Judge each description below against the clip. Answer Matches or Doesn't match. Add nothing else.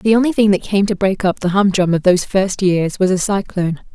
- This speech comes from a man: Doesn't match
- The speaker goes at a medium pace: Doesn't match